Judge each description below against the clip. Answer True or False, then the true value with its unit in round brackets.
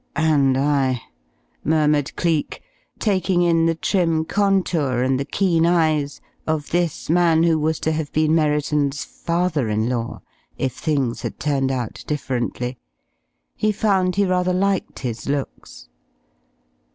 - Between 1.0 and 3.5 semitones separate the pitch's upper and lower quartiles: False (4.2 semitones)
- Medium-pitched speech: True (155 Hz)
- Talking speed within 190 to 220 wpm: False (135 wpm)